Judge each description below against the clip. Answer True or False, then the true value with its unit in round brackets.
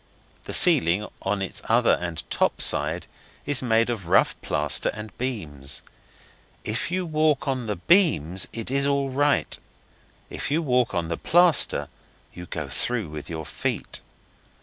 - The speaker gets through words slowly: False (150 wpm)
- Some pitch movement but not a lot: False (8.5 semitones)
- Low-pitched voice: True (115 Hz)